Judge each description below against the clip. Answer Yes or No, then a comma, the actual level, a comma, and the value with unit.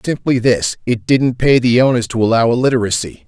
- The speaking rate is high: No, average, 185 wpm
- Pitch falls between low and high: No, low, 120 Hz